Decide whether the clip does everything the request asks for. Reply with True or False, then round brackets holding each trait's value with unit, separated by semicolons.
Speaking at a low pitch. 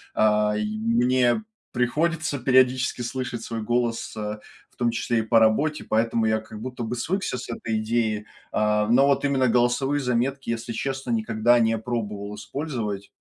True (120 Hz)